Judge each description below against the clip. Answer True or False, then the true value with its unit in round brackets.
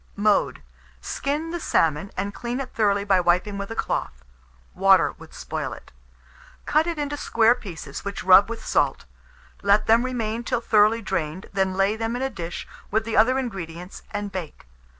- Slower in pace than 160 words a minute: False (175 wpm)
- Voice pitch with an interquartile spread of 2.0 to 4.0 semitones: True (3.7 semitones)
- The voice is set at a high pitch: True (205 Hz)